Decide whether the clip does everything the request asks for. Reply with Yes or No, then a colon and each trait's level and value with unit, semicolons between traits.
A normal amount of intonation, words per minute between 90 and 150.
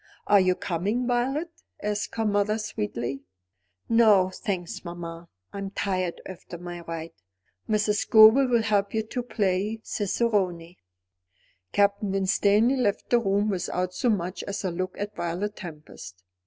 Yes: average, 3.4 semitones; average, 140 wpm